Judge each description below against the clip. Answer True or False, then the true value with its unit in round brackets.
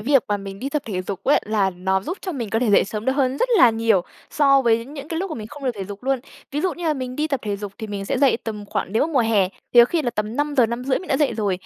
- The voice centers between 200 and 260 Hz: True (235 Hz)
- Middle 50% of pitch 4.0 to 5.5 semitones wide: True (5.2 semitones)